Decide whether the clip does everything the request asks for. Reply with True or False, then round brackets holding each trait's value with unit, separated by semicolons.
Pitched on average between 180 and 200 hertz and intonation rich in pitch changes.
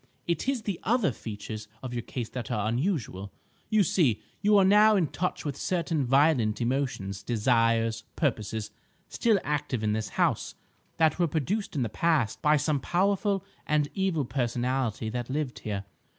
False (135 Hz; 7.1 semitones)